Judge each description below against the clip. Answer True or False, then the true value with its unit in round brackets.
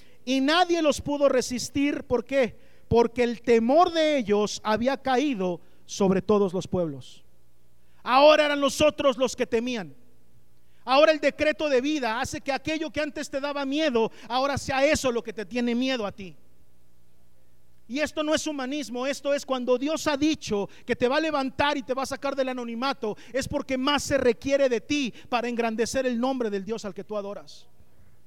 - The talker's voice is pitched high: True (255 Hz)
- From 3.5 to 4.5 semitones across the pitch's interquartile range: False (5.4 semitones)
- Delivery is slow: False (185 wpm)